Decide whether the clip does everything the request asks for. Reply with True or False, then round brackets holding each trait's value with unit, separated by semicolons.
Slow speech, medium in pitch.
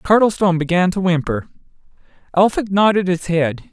True (130 wpm; 180 Hz)